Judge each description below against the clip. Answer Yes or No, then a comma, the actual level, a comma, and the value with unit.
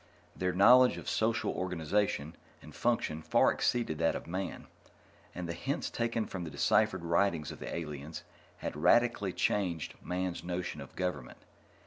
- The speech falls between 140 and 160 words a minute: Yes, average, 150 wpm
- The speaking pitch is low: Yes, very low, 90 Hz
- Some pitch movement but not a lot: Yes, average, 4.1 semitones